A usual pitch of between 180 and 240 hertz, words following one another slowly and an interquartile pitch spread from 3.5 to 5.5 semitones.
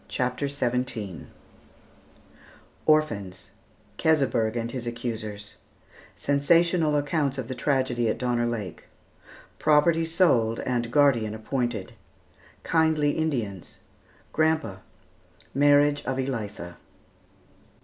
No: low, 130 Hz; slow, 90 wpm; average, 4.5 semitones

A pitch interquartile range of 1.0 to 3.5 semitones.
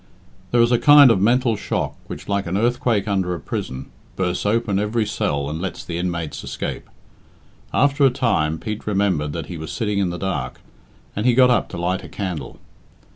No: average, 5.2 semitones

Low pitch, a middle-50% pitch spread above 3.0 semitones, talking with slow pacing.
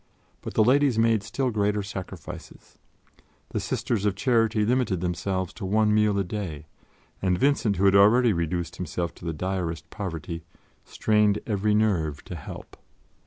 No: low, 100 Hz; average, 3.6 semitones; average, 155 wpm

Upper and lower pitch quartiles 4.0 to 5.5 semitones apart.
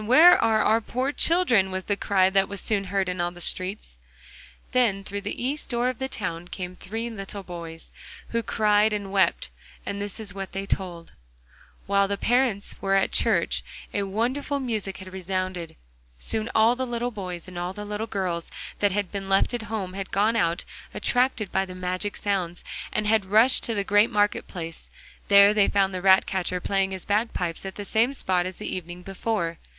No: average, 2.9 semitones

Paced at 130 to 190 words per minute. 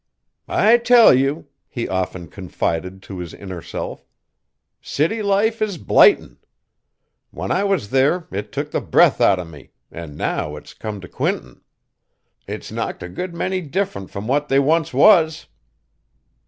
Yes: average, 155 wpm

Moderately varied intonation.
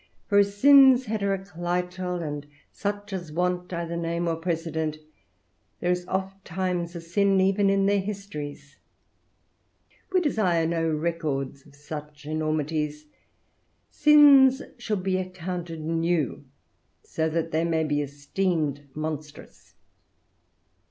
Yes: average, 3.8 semitones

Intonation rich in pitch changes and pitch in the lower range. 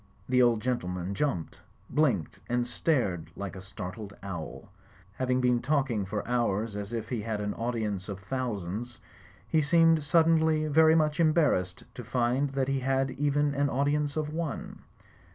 Yes: wide, 6.1 semitones; low, 125 Hz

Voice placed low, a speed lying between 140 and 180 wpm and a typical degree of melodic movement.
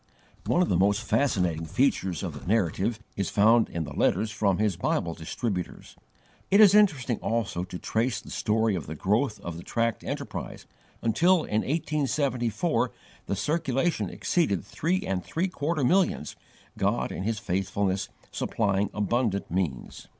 No: low, 110 Hz; average, 150 wpm; wide, 6.5 semitones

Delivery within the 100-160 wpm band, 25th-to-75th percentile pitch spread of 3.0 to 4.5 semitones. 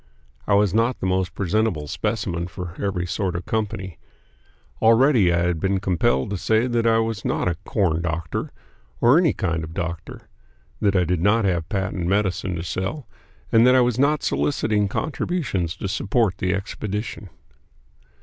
No: average, 170 wpm; average, 4.2 semitones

